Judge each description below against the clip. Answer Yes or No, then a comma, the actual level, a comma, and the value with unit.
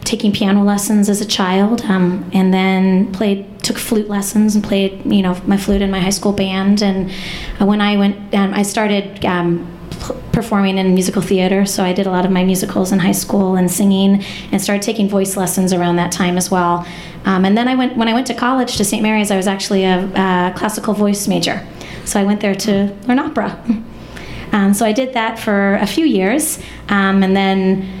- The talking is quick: Yes, fast, 210 wpm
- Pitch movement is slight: Yes, narrow, 1.8 semitones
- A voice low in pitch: No, high, 200 Hz